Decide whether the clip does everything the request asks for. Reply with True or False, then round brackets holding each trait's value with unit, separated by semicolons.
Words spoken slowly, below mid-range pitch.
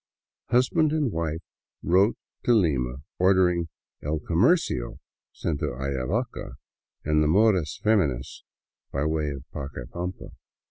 True (125 wpm; 80 Hz)